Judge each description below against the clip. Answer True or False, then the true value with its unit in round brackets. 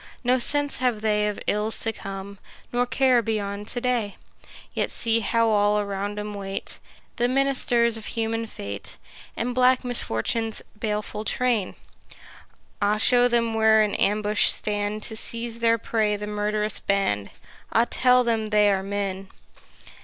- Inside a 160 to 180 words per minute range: False (150 wpm)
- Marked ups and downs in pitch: False (2.4 semitones)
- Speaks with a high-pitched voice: True (215 Hz)